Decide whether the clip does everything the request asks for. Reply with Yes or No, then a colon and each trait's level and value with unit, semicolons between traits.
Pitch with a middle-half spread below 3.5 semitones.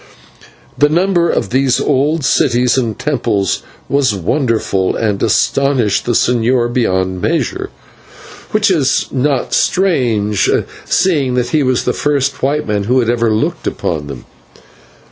No: average, 4.8 semitones